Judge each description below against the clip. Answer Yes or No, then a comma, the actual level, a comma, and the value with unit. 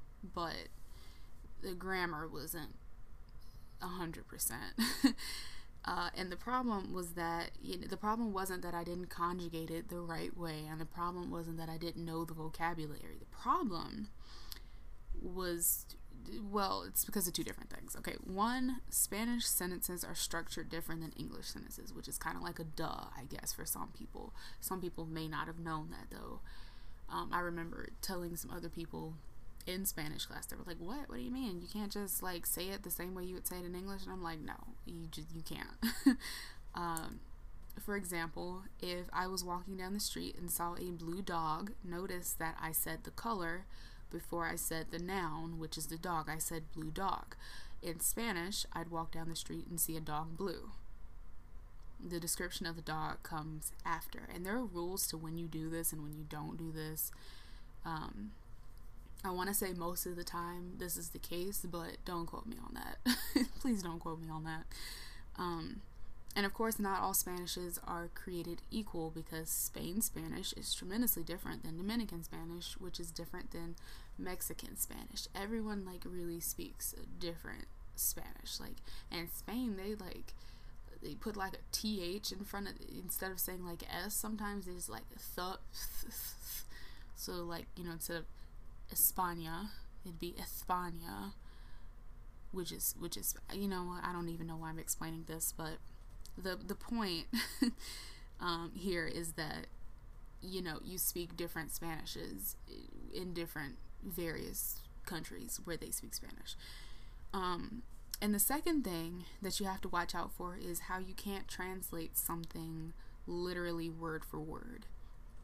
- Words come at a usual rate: Yes, average, 175 wpm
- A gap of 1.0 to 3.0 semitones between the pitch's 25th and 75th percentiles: Yes, average, 2.7 semitones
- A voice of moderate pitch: Yes, medium, 175 Hz